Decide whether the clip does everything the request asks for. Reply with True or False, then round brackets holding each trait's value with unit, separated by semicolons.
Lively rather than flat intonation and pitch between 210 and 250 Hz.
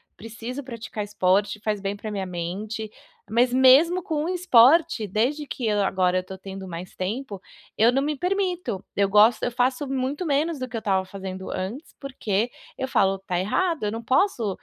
True (5.7 semitones; 225 Hz)